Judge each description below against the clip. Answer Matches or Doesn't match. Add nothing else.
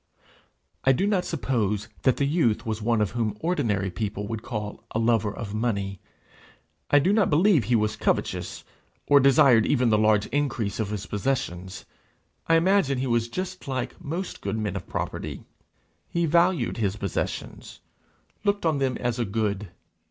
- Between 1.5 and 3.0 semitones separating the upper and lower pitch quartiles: Doesn't match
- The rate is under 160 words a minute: Doesn't match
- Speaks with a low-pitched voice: Matches